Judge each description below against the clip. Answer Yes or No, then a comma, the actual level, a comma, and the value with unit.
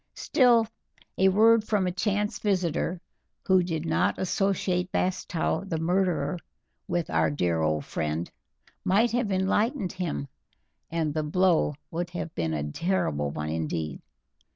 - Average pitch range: No, wide, 5.8 semitones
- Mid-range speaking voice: Yes, medium, 180 Hz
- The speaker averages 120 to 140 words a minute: Yes, slow, 135 wpm